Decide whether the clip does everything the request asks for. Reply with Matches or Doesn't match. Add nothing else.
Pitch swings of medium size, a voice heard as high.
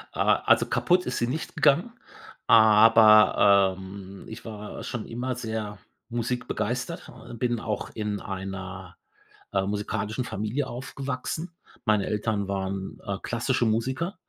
Doesn't match